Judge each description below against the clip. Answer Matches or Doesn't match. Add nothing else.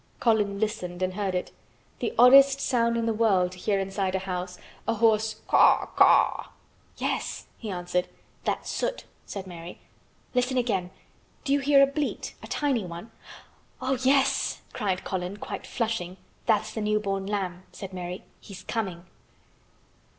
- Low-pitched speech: Doesn't match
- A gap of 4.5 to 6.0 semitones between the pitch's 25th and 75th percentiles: Doesn't match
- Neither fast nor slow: Matches